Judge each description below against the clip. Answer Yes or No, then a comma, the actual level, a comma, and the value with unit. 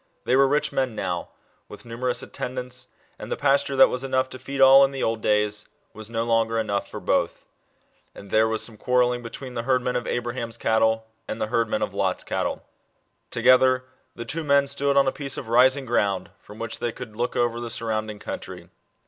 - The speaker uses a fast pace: Yes, fast, 210 wpm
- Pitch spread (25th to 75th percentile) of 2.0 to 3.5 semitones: Yes, average, 2.7 semitones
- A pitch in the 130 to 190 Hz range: No, low, 120 Hz